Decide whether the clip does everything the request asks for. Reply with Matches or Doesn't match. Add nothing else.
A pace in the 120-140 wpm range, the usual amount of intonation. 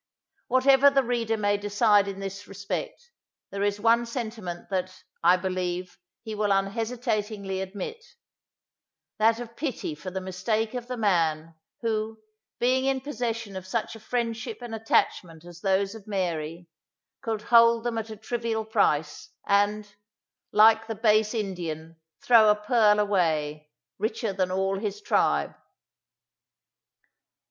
Matches